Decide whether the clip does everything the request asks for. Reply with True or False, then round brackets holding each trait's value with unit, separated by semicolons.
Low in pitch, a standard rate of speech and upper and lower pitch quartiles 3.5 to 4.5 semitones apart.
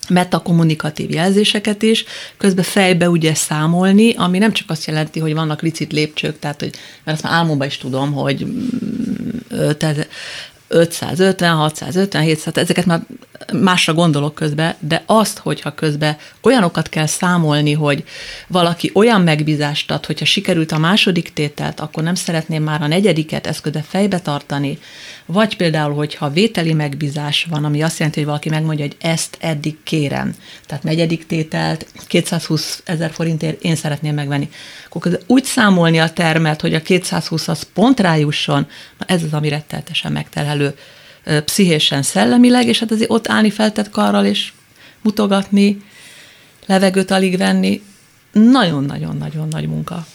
False (165 Hz; 140 wpm; 4.0 semitones)